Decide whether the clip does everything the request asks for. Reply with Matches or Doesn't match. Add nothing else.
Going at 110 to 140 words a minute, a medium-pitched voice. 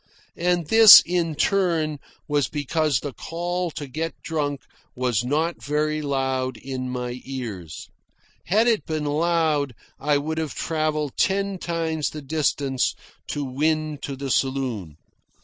Matches